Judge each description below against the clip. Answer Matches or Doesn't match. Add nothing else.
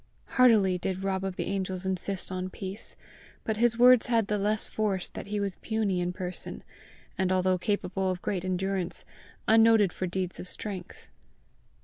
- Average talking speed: Matches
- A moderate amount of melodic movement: Doesn't match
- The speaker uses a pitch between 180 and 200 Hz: Matches